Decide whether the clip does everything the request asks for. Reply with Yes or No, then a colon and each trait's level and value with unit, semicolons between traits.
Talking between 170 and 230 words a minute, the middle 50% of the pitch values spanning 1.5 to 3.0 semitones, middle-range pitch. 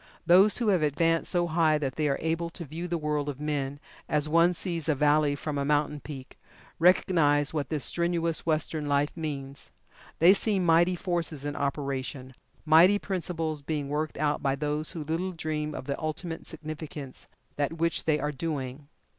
Yes: average, 180 wpm; narrow, 2.4 semitones; medium, 155 Hz